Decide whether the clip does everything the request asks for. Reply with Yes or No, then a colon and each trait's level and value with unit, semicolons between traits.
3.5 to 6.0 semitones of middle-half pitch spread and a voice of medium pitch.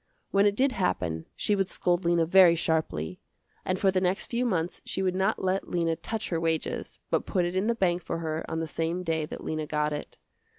No: average, 3.0 semitones; medium, 175 Hz